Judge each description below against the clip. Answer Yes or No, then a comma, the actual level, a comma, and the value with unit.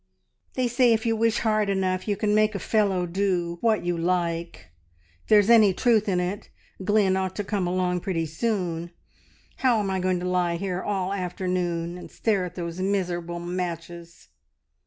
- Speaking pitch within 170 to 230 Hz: Yes, medium, 185 Hz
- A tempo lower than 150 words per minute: No, average, 180 wpm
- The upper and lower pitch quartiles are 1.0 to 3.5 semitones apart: Yes, average, 3.0 semitones